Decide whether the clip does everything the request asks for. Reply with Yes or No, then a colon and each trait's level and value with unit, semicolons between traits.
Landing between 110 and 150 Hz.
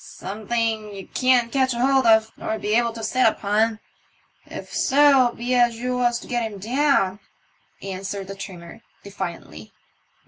No: high, 225 Hz